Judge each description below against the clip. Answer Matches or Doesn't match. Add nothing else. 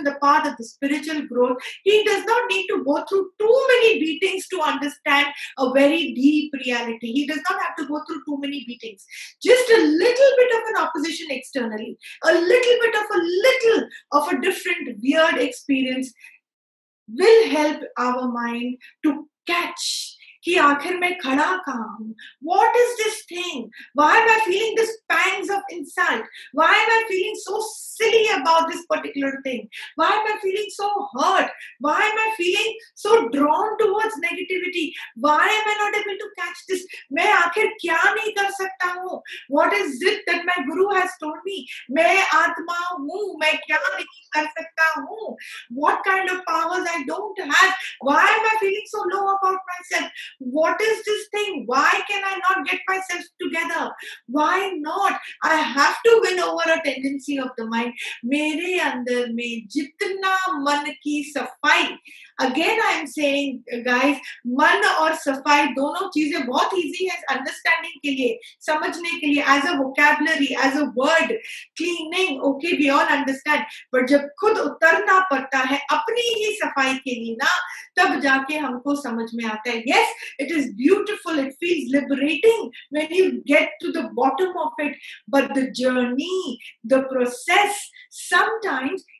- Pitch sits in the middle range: Doesn't match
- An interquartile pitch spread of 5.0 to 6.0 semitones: Matches